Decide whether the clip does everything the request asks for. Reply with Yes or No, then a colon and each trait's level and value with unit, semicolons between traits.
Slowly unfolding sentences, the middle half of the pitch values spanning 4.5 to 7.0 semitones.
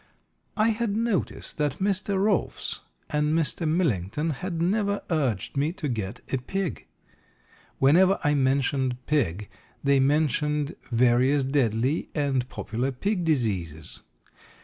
Yes: slow, 120 wpm; wide, 5.4 semitones